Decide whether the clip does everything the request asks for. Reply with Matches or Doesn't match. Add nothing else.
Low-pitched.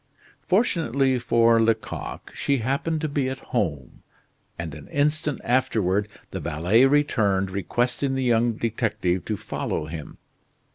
Matches